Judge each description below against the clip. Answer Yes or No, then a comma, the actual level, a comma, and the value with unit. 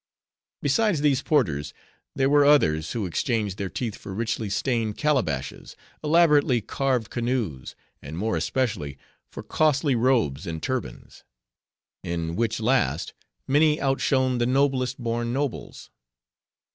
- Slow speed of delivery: Yes, slow, 120 wpm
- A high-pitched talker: No, low, 120 Hz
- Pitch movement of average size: No, wide, 5.8 semitones